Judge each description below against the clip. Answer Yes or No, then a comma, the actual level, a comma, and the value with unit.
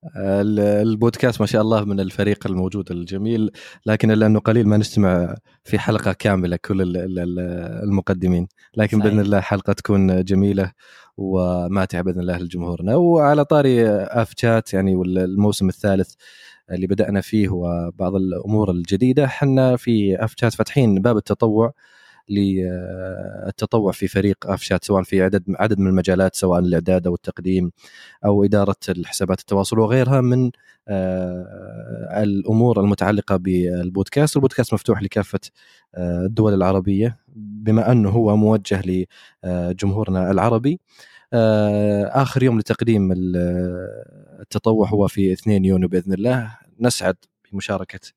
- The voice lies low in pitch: Yes, low, 100 Hz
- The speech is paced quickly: No, average, 115 wpm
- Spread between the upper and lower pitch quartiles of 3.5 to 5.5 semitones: No, average, 2.9 semitones